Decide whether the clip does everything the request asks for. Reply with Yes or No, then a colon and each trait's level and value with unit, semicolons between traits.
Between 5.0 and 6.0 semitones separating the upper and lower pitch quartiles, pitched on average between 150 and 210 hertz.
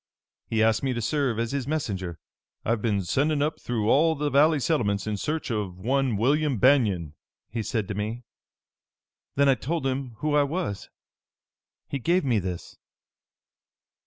No: average, 5.3 semitones; low, 125 Hz